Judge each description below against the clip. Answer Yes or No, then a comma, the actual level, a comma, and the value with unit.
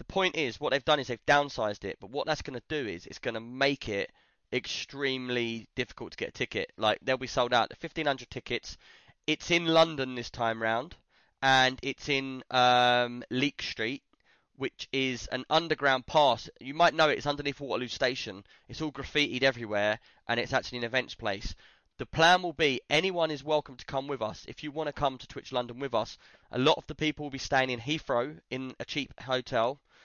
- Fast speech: Yes, fast, 210 wpm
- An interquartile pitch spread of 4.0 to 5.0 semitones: No, average, 3.3 semitones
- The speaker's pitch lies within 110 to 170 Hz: Yes, low, 135 Hz